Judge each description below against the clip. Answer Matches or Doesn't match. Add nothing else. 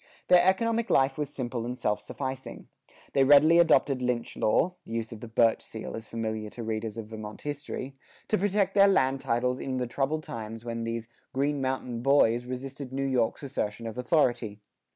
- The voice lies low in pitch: Matches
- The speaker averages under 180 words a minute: Doesn't match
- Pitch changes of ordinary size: Matches